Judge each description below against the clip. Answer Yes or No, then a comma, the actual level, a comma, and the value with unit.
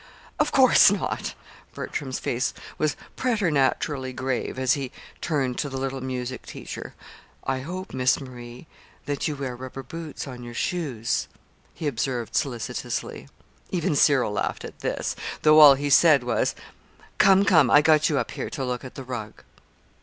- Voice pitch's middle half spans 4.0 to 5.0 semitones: No, average, 3.0 semitones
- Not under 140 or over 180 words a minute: Yes, average, 160 wpm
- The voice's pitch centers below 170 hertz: Yes, low, 135 Hz